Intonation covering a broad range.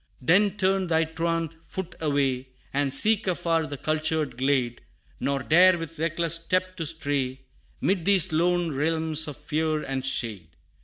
No: average, 3.2 semitones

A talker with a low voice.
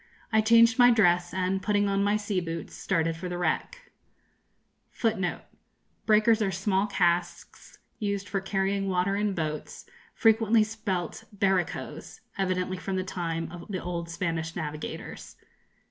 No: high, 190 Hz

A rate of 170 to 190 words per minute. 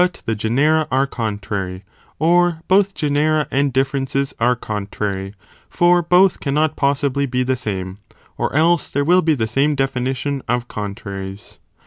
No: average, 140 wpm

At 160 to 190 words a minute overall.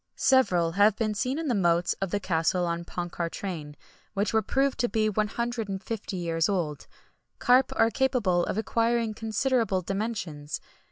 No: average, 150 wpm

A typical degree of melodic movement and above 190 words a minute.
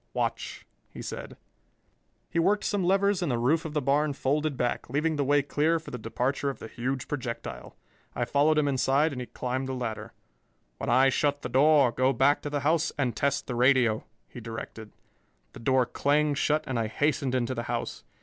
Yes: average, 3.3 semitones; average, 200 wpm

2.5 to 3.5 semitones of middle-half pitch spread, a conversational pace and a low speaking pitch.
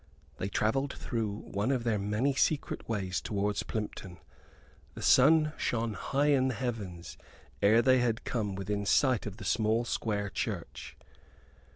No: average, 4.0 semitones; average, 150 wpm; low, 110 Hz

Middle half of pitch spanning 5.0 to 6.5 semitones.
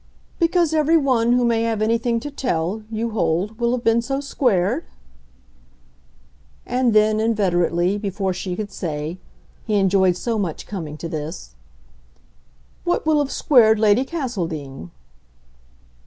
Yes: average, 5.3 semitones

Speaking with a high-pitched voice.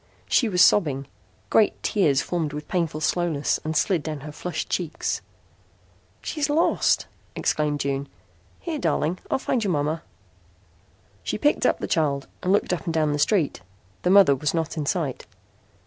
No: medium, 160 Hz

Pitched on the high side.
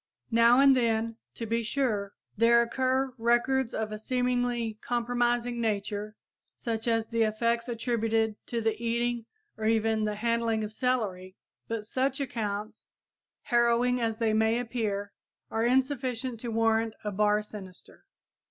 Yes: high, 230 Hz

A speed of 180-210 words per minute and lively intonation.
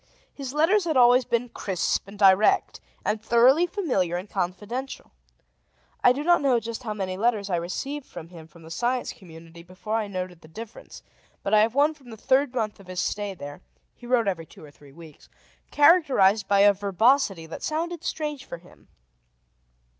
Yes: average, 185 wpm; wide, 6.1 semitones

